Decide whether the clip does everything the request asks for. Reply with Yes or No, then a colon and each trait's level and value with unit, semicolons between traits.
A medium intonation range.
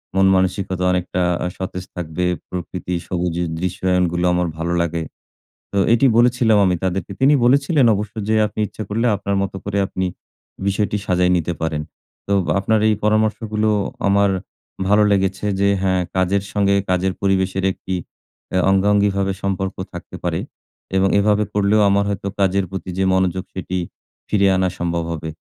No: narrow, 1.9 semitones